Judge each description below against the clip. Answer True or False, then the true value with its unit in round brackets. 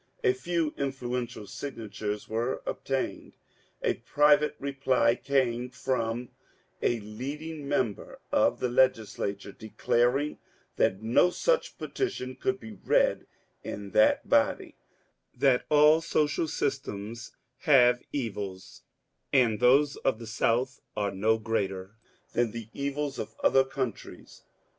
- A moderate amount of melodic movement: True (4.2 semitones)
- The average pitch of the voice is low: True (125 Hz)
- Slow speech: True (120 wpm)